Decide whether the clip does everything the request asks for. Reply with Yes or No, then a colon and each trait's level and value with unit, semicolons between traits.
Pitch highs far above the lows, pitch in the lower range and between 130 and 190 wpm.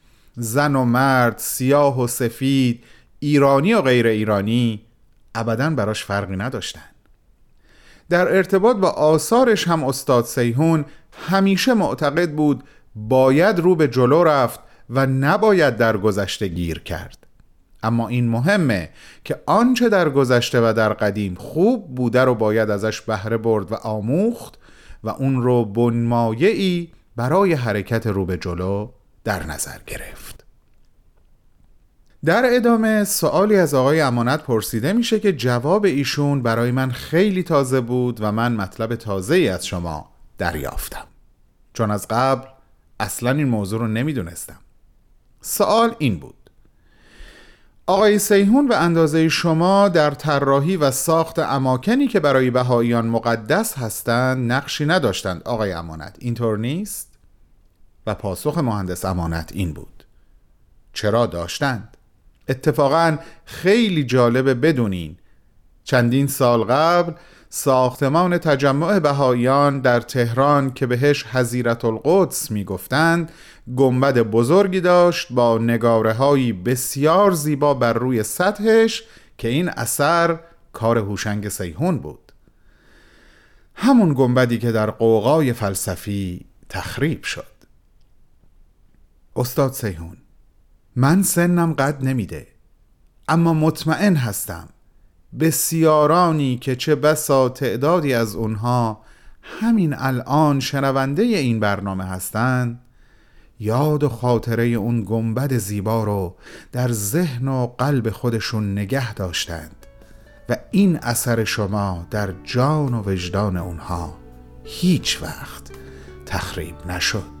No: wide, 6.0 semitones; low, 125 Hz; average, 115 wpm